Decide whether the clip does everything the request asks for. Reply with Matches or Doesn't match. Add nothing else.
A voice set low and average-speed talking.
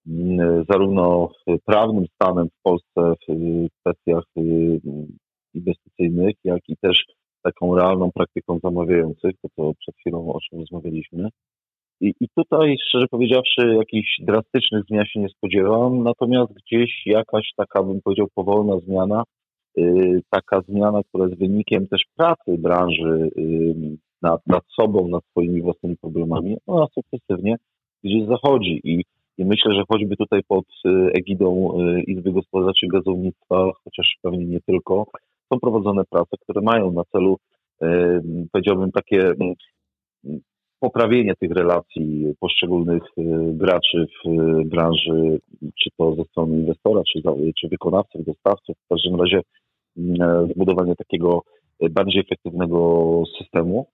Matches